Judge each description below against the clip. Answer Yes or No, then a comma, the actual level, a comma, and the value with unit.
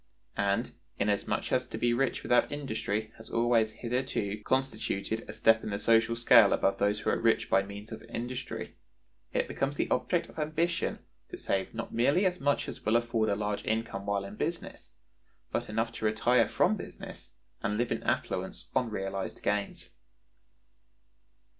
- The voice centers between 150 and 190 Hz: No, low, 115 Hz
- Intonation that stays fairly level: No, average, 3.0 semitones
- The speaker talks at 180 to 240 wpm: No, average, 170 wpm